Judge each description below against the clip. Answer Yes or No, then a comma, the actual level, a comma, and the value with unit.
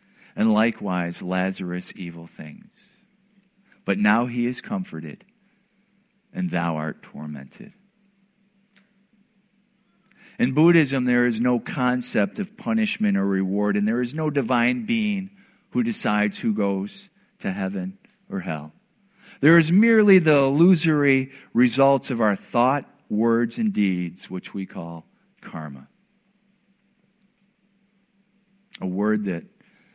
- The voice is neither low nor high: Yes, medium, 170 Hz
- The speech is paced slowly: Yes, slow, 115 wpm